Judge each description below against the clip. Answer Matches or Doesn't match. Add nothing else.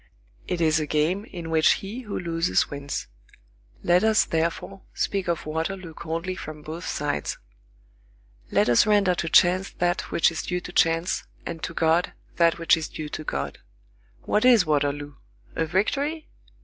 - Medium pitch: Matches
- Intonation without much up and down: Doesn't match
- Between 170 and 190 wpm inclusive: Doesn't match